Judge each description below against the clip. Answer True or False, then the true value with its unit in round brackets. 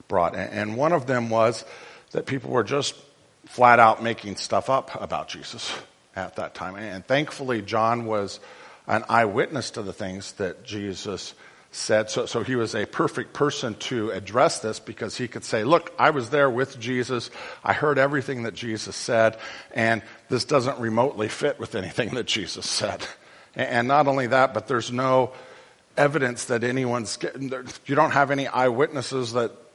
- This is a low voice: True (120 Hz)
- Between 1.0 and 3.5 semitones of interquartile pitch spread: True (3.2 semitones)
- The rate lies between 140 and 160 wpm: False (175 wpm)